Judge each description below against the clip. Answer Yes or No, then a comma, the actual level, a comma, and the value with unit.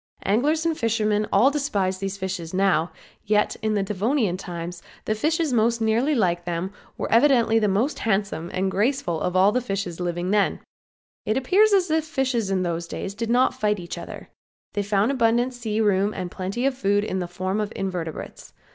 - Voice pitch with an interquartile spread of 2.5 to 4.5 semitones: Yes, average, 4.2 semitones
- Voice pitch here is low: No, high, 210 Hz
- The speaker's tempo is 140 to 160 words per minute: No, average, 180 wpm